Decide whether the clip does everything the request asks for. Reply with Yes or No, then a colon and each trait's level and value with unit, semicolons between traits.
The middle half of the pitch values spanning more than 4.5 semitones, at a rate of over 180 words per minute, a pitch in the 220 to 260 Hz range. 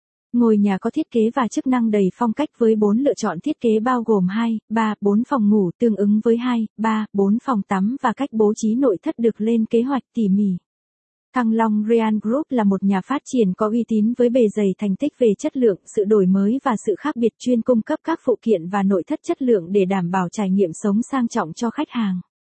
No: average, 3.5 semitones; average, 245 wpm; high, 225 Hz